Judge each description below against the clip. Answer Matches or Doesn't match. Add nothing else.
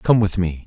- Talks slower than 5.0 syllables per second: Matches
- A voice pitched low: Matches